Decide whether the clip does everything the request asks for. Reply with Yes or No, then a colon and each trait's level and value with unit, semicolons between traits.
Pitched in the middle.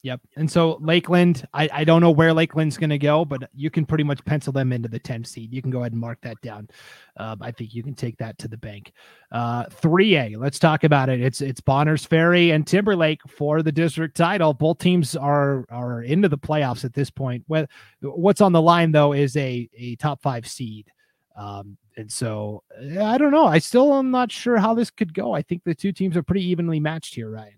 Yes: medium, 150 Hz